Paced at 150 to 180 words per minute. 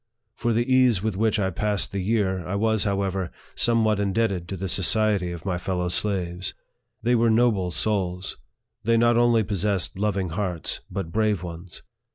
Yes: average, 175 wpm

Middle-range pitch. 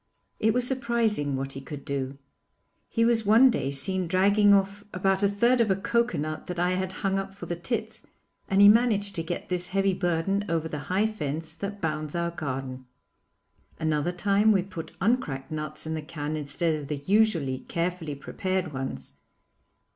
Yes: medium, 180 Hz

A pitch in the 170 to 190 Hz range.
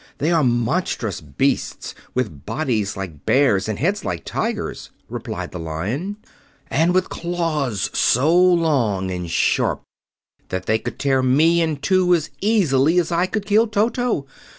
No: medium, 145 Hz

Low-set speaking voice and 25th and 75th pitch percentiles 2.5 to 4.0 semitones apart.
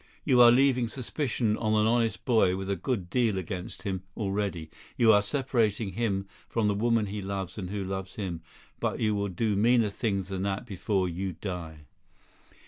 Yes: low, 105 Hz; average, 3.2 semitones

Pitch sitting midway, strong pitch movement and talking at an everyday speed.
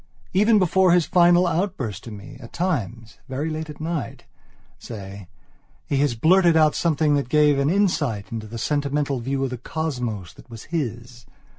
Yes: medium, 145 Hz; wide, 5.9 semitones; average, 170 wpm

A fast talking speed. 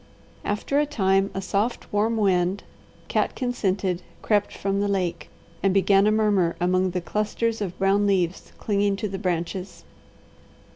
No: average, 150 wpm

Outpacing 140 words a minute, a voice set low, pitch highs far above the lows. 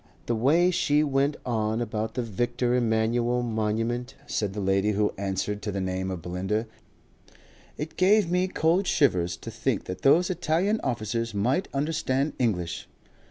Yes: average, 155 wpm; low, 120 Hz; wide, 5.9 semitones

